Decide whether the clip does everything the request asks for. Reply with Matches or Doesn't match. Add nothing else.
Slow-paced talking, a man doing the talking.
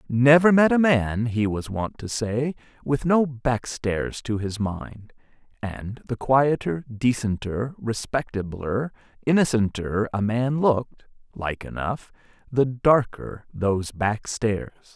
Matches